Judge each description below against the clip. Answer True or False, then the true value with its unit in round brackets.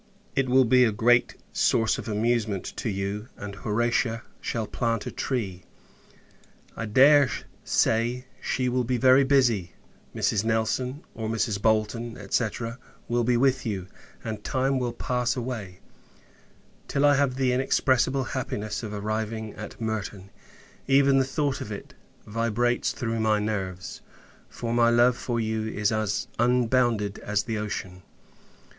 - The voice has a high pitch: False (115 Hz)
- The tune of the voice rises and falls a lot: False (2.9 semitones)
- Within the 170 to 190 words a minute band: False (145 wpm)